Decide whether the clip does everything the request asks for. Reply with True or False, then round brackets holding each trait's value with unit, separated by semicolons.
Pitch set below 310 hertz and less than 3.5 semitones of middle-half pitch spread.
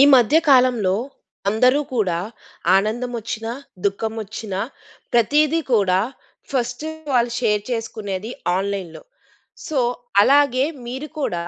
False (230 Hz; 4.1 semitones)